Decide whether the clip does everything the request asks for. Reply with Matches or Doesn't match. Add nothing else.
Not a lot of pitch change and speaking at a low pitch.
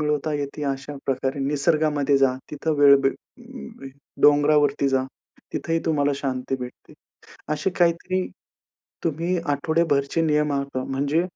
Doesn't match